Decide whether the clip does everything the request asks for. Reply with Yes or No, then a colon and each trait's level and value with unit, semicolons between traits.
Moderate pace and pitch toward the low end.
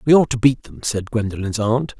No: fast, 240 wpm; low, 120 Hz